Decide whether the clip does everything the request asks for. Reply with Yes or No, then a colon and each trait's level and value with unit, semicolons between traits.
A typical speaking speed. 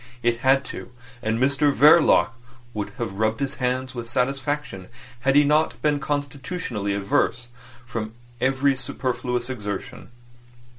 No: slow, 120 wpm